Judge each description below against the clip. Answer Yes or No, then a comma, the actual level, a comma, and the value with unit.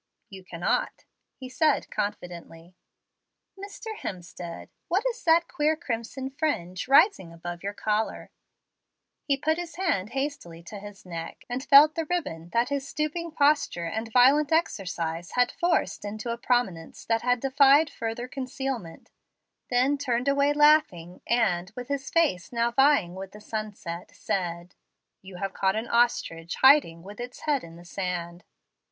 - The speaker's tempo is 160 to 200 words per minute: No, average, 145 wpm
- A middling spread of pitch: No, wide, 7.9 semitones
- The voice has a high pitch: Yes, high, 235 Hz